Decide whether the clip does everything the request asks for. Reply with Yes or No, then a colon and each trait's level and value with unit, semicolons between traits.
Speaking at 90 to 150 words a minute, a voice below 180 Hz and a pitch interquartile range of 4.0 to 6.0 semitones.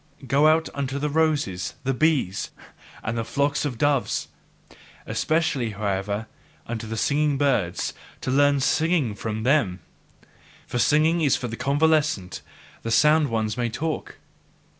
Yes: average, 140 wpm; low, 135 Hz; average, 5.1 semitones